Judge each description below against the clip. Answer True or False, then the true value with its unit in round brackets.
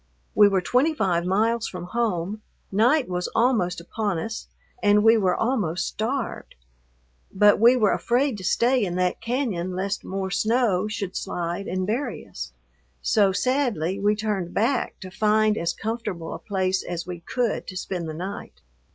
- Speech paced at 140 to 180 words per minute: True (165 wpm)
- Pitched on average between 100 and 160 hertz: False (205 Hz)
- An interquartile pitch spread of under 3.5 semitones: False (4.0 semitones)